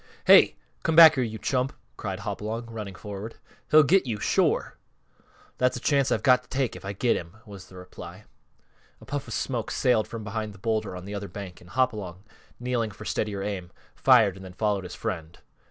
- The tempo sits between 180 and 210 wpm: Yes, average, 200 wpm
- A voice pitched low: Yes, low, 110 Hz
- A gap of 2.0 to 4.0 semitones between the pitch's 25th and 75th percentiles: No, average, 4.5 semitones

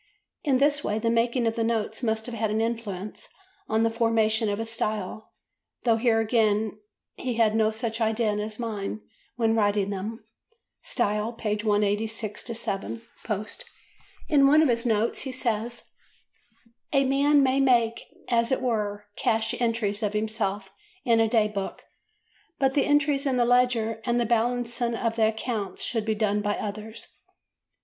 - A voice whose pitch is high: Yes, high, 225 Hz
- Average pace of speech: Yes, average, 160 wpm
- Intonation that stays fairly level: Yes, narrow, 2.0 semitones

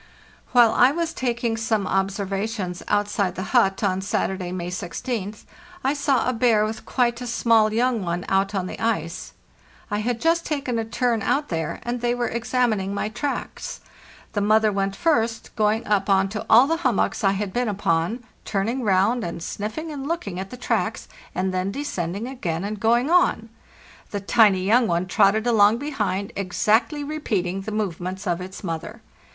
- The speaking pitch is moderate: No, high, 215 Hz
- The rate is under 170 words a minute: No, average, 175 wpm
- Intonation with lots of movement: No, average, 3.9 semitones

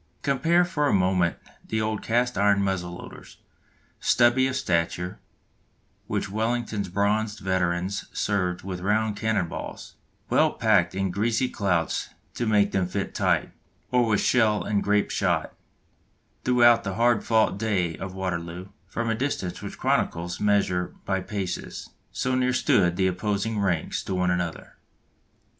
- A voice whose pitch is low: Yes, low, 100 Hz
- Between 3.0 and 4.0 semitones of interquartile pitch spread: Yes, average, 3.5 semitones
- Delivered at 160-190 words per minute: No, average, 150 wpm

